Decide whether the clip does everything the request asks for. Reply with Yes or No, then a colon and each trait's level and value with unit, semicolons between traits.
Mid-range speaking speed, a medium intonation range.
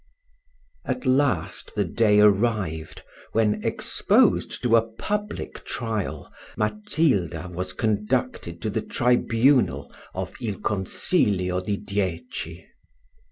No: slow, 100 wpm; average, 3.9 semitones